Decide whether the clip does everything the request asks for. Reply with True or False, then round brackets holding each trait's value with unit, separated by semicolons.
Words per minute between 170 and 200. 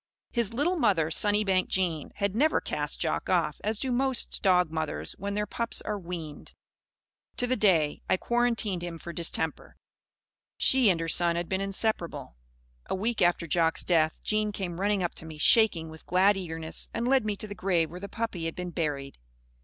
True (190 wpm)